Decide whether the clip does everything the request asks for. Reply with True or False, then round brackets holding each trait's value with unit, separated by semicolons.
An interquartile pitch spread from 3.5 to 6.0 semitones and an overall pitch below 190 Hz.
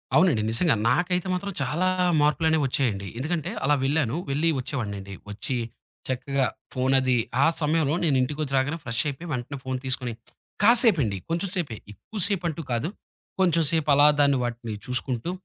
True (4.6 semitones; 140 Hz)